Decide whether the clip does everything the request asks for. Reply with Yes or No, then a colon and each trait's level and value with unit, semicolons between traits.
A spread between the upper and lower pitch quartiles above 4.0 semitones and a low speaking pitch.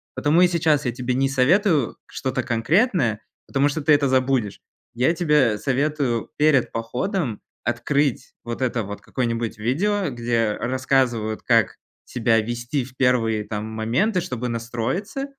Yes: average, 4.4 semitones; low, 130 Hz